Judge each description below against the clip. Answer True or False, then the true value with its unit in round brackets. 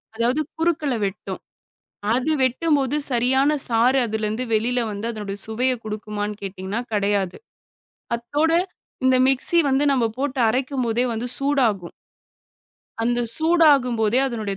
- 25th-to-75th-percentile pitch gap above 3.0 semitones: True (3.9 semitones)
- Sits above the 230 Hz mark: True (240 Hz)